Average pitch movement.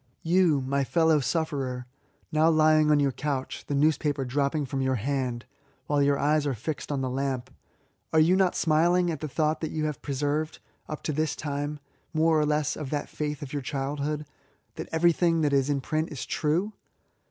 No: narrow, 2.1 semitones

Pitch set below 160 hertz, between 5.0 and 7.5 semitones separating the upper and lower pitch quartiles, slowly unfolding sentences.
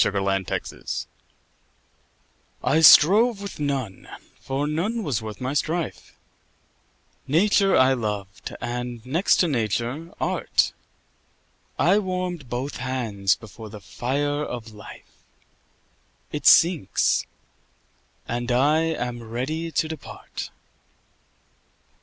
Yes: low, 135 Hz; wide, 5.6 semitones; slow, 100 wpm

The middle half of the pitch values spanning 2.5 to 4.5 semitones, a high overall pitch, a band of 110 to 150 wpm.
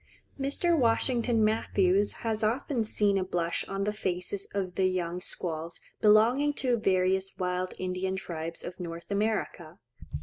Yes: average, 3.5 semitones; high, 195 Hz; average, 140 wpm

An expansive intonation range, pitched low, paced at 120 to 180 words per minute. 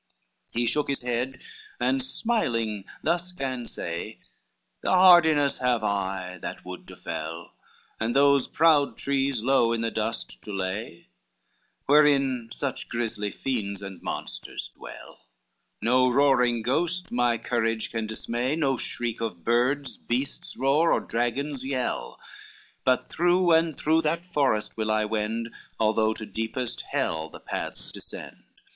No: average, 4.3 semitones; low, 120 Hz; average, 140 wpm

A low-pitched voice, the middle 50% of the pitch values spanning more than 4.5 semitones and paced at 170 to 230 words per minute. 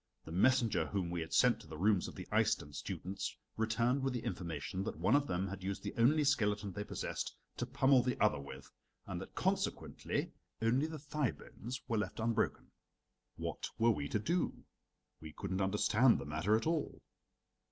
Yes: low, 105 Hz; average, 5.2 semitones; average, 185 wpm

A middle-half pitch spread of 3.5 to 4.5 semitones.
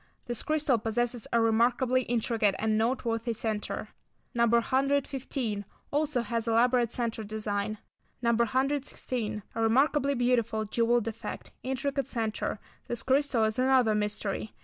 No: average, 2.8 semitones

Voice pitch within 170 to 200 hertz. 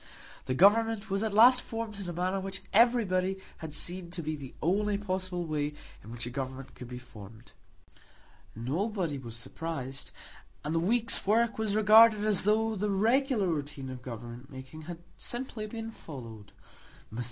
Yes: medium, 185 Hz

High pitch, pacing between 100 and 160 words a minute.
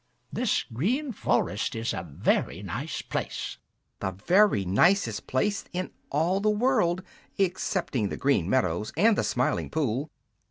No: medium, 160 Hz; slow, 135 wpm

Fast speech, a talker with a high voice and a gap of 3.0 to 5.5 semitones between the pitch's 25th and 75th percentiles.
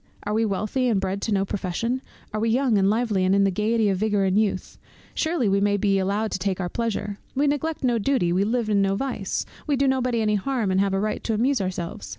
Yes: fast, 250 wpm; high, 210 Hz; average, 3.5 semitones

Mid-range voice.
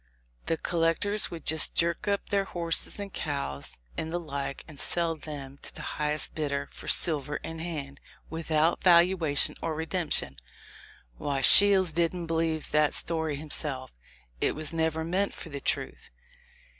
Yes: medium, 160 Hz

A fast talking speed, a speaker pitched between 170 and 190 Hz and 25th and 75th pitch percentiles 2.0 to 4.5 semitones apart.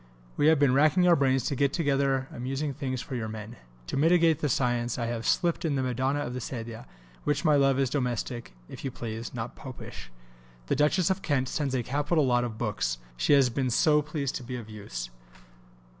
No: fast, 210 wpm; low, 130 Hz; average, 3.3 semitones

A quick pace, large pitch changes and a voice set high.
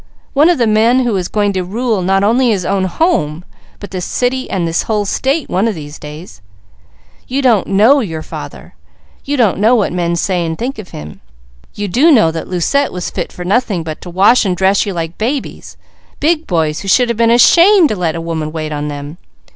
Yes: fast, 220 wpm; wide, 6.2 semitones; high, 200 Hz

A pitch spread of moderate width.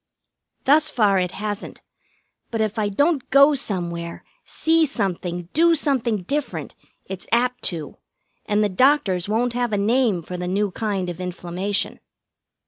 No: wide, 5.8 semitones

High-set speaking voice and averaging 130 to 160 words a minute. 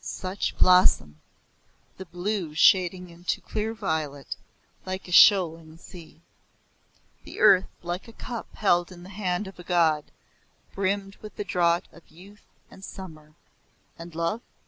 No: medium, 180 Hz; average, 140 wpm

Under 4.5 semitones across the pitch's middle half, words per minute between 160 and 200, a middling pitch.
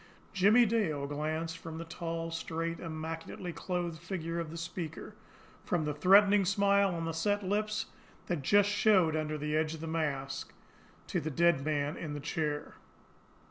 Yes: average, 3.3 semitones; average, 165 wpm; medium, 165 Hz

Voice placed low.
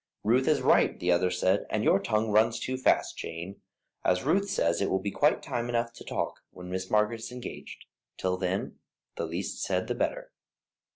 Yes: low, 105 Hz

